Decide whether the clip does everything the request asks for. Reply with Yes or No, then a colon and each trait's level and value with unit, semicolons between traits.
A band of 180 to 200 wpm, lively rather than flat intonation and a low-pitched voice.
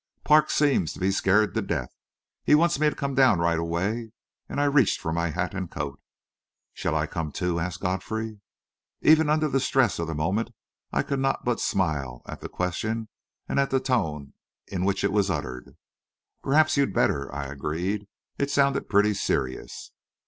Yes: average, 185 wpm; wide, 8.4 semitones; low, 100 Hz